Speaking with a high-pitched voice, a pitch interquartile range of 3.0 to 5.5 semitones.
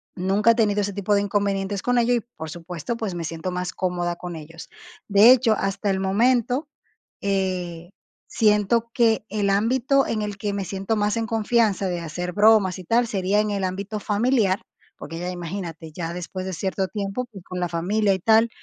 Yes: high, 200 Hz; average, 3.3 semitones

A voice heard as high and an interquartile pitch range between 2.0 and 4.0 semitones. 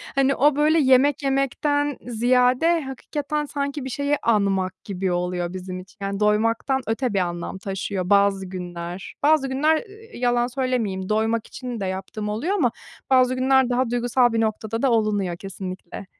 No: high, 235 Hz; wide, 5.6 semitones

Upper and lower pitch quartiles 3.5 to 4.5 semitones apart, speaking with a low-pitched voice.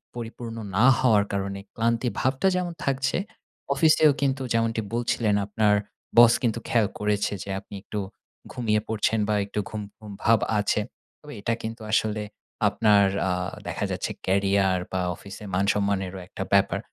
No: average, 2.7 semitones; low, 110 Hz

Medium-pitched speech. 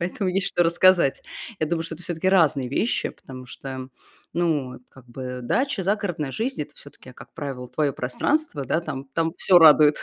Yes: medium, 155 Hz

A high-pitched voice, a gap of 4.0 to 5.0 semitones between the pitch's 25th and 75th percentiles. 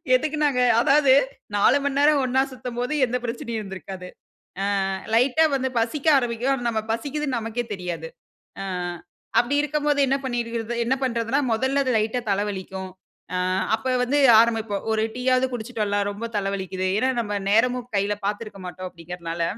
Yes: high, 235 Hz; average, 4.3 semitones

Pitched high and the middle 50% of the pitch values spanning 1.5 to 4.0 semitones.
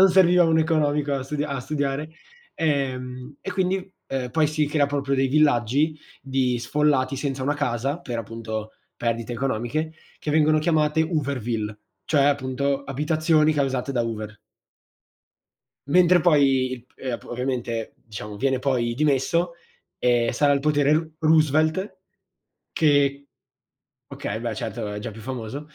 No: medium, 140 Hz; average, 3.6 semitones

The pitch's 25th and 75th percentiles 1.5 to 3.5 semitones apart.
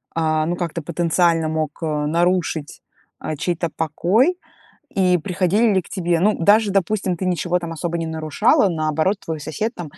Yes: average, 2.9 semitones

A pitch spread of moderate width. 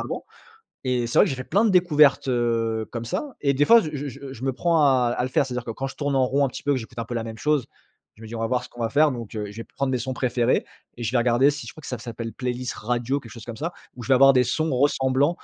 Yes: average, 3.1 semitones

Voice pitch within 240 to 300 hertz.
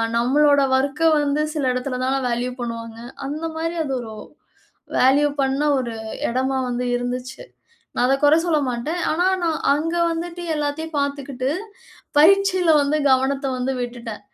Yes: very high, 275 Hz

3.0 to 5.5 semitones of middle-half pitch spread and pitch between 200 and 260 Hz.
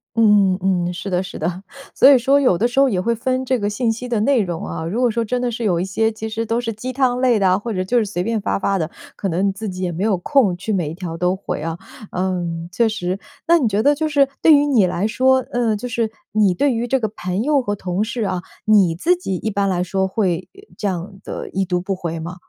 Yes: average, 4.7 semitones; high, 205 Hz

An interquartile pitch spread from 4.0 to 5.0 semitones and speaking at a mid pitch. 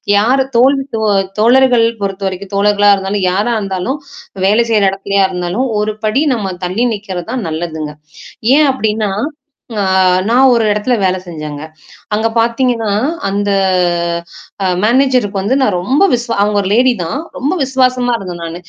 No: average, 4.3 semitones; high, 210 Hz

